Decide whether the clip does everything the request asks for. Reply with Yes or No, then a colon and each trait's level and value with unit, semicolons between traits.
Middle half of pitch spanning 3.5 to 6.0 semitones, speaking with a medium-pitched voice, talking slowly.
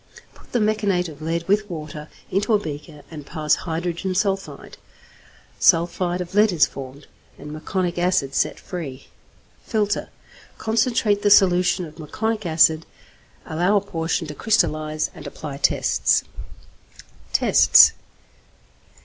Yes: average, 4.5 semitones; medium, 175 Hz; slow, 125 wpm